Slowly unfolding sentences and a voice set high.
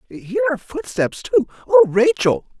No: slow, 115 wpm; medium, 170 Hz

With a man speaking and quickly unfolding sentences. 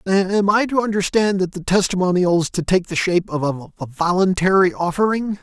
No: male; average, 175 wpm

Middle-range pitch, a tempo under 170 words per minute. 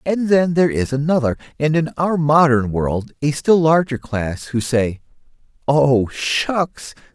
Yes: medium, 145 Hz; average, 150 wpm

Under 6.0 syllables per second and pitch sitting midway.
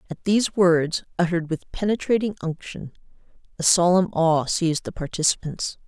Yes: 5.3 syllables/s; medium, 175 Hz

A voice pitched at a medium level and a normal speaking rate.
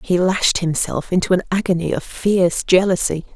Yes: medium, 180 Hz; average, 160 wpm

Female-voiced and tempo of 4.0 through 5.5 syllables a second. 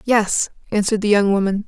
No: female; 5.9 syllables/s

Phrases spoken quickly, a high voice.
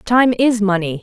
No: average, 175 wpm; high, 210 Hz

